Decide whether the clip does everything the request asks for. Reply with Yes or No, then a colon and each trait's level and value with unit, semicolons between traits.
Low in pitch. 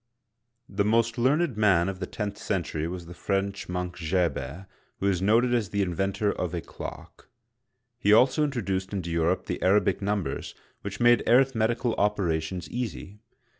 Yes: low, 100 Hz